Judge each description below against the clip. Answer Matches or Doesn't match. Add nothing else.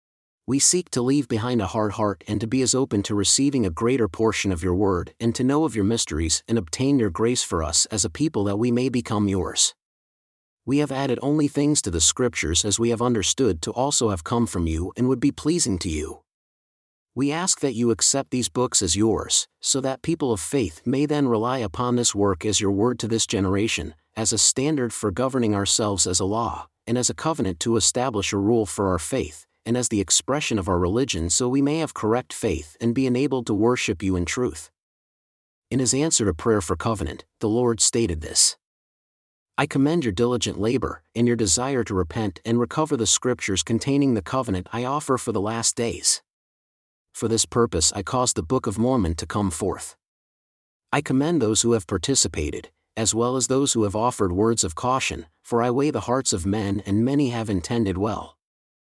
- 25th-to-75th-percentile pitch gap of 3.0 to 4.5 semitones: Matches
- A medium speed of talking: Doesn't match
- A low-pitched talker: Matches